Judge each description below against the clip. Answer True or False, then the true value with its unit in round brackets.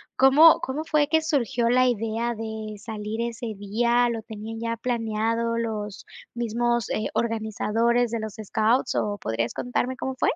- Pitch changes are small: True (1.9 semitones)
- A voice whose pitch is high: True (230 Hz)